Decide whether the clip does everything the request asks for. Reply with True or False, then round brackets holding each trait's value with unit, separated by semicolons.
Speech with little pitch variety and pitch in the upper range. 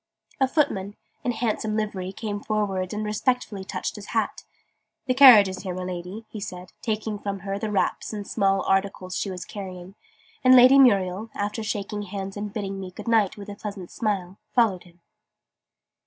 True (2.3 semitones; 205 Hz)